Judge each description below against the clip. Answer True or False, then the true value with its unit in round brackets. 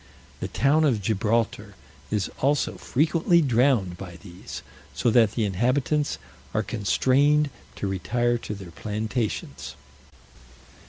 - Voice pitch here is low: True (115 Hz)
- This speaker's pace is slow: True (115 wpm)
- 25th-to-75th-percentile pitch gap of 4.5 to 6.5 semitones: True (5.3 semitones)